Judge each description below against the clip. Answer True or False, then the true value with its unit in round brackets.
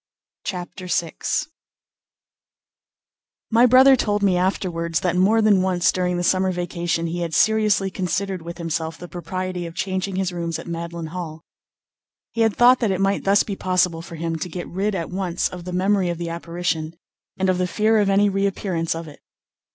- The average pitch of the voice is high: False (180 Hz)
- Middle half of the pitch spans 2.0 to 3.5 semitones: True (2.5 semitones)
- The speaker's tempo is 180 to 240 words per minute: True (185 wpm)